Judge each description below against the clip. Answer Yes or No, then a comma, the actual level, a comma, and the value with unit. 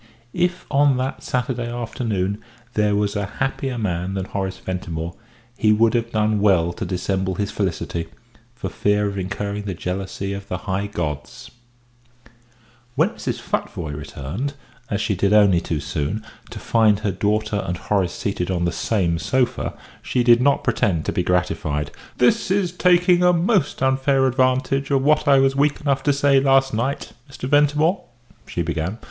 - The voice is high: No, low, 105 Hz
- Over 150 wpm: Yes, average, 165 wpm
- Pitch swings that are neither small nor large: No, wide, 6.2 semitones